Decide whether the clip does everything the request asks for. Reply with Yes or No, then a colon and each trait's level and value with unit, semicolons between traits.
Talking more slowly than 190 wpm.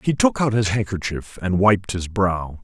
No: fast, 205 wpm